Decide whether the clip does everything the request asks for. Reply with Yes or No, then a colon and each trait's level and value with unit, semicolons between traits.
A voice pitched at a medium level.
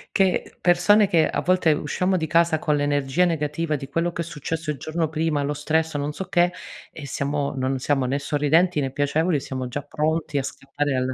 Yes: medium, 150 Hz